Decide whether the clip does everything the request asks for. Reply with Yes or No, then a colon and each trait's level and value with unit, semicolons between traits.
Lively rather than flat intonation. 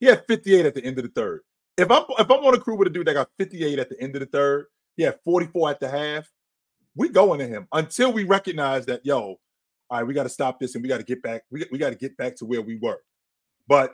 Yes: wide, 7.0 semitones